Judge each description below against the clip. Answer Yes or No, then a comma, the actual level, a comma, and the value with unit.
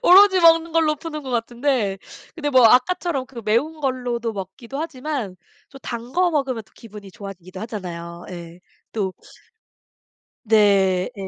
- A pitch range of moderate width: No, wide, 6.9 semitones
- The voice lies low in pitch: No, high, 240 Hz